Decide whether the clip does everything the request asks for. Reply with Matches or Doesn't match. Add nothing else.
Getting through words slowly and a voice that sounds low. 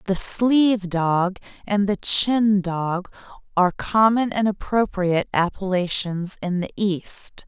Doesn't match